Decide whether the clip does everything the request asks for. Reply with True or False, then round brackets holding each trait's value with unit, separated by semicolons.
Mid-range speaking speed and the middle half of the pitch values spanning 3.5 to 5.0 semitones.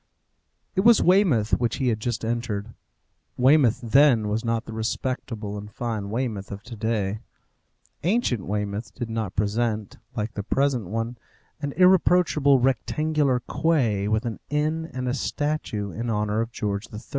True (155 wpm; 4.6 semitones)